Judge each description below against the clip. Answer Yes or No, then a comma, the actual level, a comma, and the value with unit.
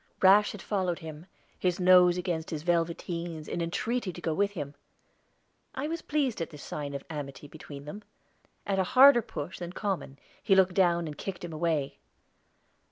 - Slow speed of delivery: No, average, 175 wpm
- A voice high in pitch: No, medium, 175 Hz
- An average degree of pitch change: Yes, average, 3.6 semitones